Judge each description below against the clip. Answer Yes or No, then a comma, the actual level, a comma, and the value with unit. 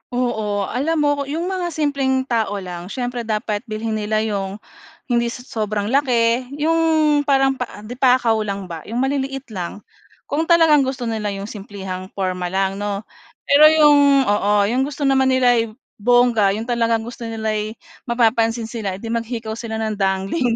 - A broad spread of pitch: No, average, 4.1 semitones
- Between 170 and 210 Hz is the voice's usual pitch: No, high, 230 Hz